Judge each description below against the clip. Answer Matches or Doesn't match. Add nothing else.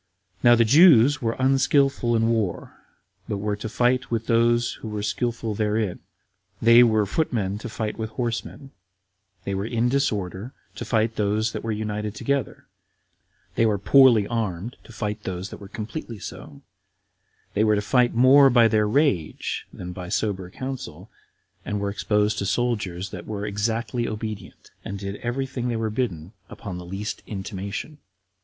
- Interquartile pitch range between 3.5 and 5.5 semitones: Doesn't match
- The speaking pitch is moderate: Doesn't match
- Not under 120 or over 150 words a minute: Doesn't match